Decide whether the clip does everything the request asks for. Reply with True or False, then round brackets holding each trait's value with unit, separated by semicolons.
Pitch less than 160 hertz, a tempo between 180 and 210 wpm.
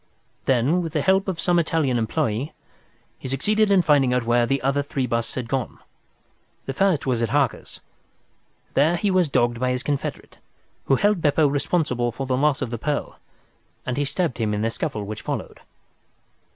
True (135 Hz; 185 wpm)